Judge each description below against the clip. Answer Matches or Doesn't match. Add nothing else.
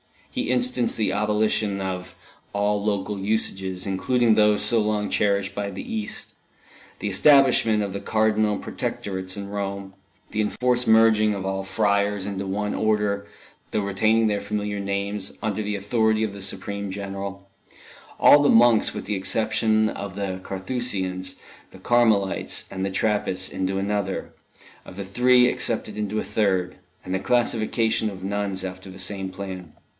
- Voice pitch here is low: Matches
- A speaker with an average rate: Matches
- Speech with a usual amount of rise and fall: Doesn't match